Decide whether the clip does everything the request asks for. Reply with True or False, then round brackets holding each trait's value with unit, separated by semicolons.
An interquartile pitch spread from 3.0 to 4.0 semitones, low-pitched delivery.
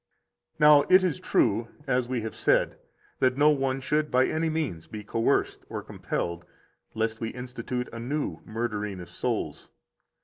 False (4.6 semitones; 125 Hz)